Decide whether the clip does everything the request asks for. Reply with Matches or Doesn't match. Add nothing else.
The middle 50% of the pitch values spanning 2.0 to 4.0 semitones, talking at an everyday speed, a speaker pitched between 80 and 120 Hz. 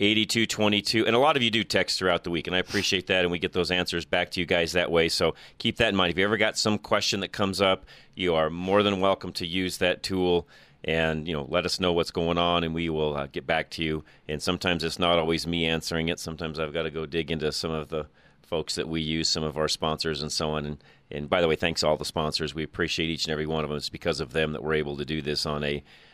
Doesn't match